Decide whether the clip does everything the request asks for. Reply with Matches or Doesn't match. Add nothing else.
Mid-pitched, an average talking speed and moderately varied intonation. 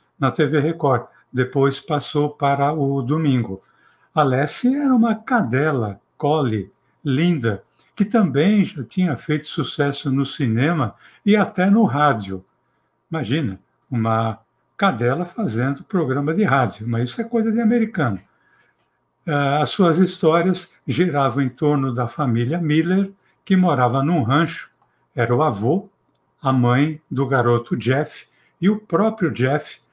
Doesn't match